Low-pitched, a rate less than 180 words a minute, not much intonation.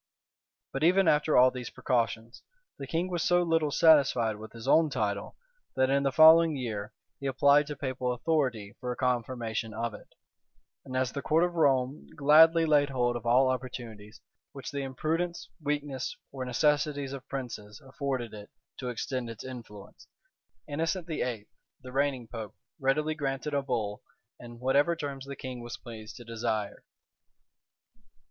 No: low, 130 Hz; average, 160 wpm; average, 3.8 semitones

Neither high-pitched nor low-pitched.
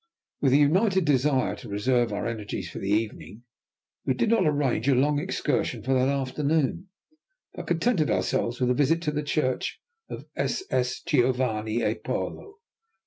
No: low, 130 Hz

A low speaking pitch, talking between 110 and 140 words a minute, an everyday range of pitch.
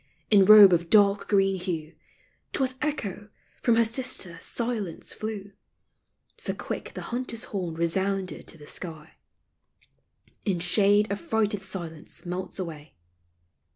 No: high, 195 Hz; slow, 135 wpm; average, 3.6 semitones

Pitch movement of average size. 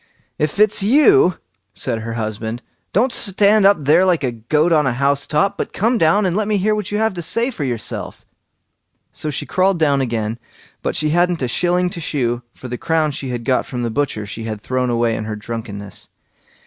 No: wide, 8.0 semitones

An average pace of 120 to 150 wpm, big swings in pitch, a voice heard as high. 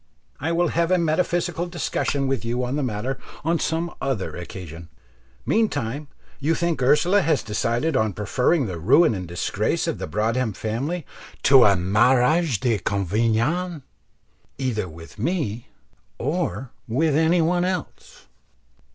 No: slow, 135 wpm; wide, 7.4 semitones; low, 135 Hz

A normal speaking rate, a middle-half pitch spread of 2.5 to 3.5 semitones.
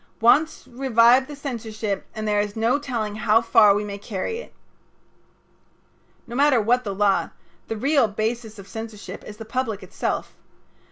Yes: average, 160 wpm; average, 3.2 semitones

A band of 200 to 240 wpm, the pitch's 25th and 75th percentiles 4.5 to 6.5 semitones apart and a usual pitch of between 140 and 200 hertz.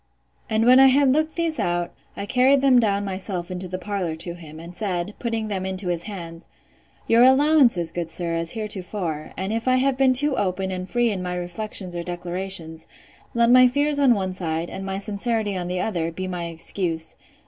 Yes: fast, 205 wpm; average, 5.2 semitones; high, 190 Hz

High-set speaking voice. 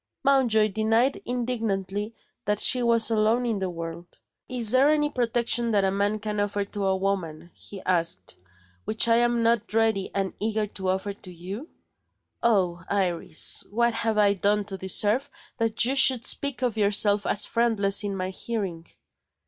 Yes: high, 210 Hz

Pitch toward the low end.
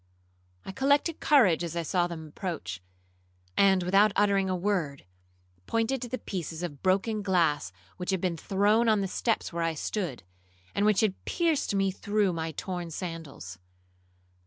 No: high, 190 Hz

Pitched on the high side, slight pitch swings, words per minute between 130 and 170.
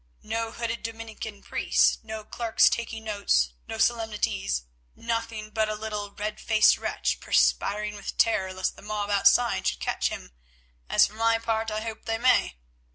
Yes: high, 220 Hz; narrow, 1.4 semitones; average, 160 wpm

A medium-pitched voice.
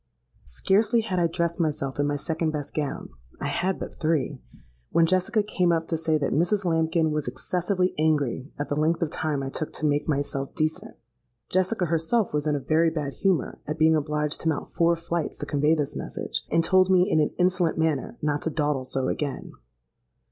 Yes: medium, 160 Hz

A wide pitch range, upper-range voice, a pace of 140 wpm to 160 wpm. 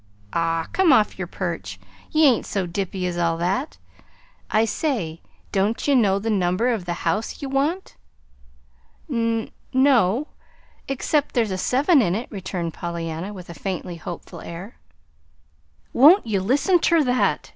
Yes: wide, 6.9 semitones; high, 210 Hz; average, 150 wpm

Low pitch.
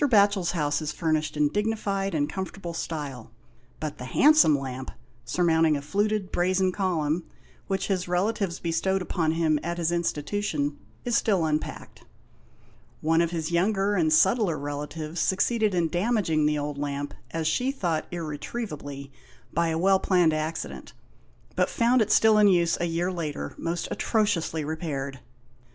No: medium, 170 Hz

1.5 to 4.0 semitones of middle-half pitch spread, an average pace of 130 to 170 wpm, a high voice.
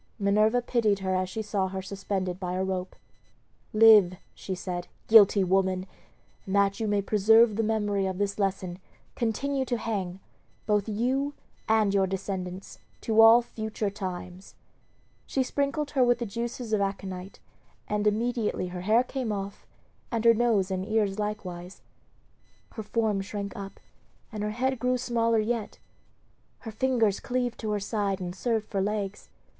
Yes: average, 2.9 semitones; average, 160 wpm; high, 210 Hz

